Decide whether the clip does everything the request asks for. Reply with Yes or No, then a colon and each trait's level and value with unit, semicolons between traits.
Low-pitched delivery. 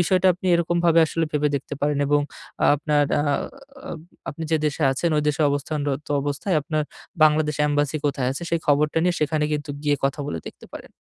No: medium, 150 Hz